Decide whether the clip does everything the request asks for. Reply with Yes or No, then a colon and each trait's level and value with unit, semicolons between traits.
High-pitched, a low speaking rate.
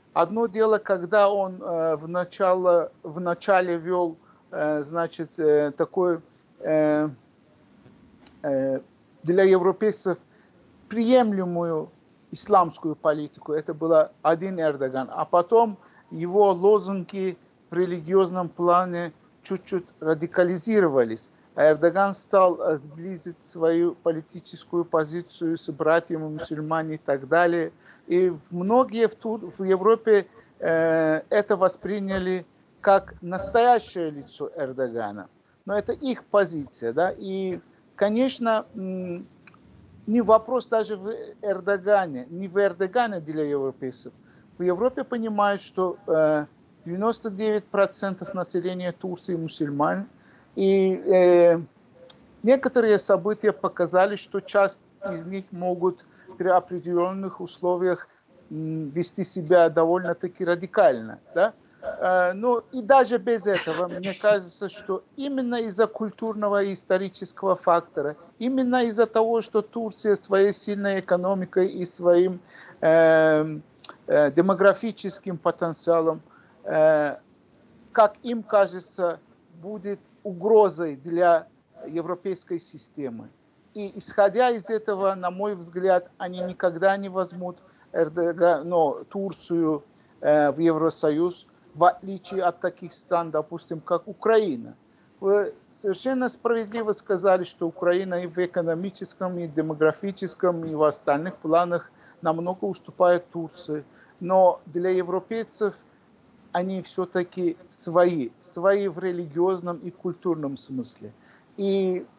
No: medium, 180 Hz; slow, 105 wpm